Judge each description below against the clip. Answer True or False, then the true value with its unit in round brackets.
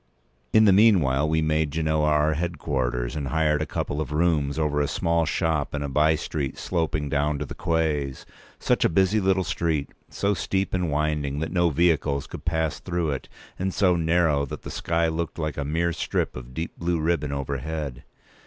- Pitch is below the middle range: True (80 Hz)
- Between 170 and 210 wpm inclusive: True (190 wpm)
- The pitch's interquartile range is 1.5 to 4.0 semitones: True (2.7 semitones)